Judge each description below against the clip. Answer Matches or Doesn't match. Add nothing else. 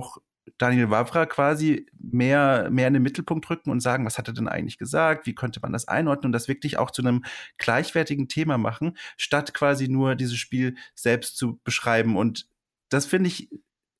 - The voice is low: Matches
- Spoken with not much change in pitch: Doesn't match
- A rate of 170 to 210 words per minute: Matches